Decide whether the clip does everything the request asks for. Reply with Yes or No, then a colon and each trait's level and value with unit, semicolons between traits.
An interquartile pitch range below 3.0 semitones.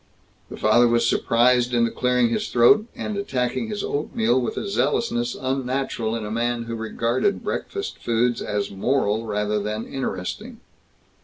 Yes: narrow, 2.4 semitones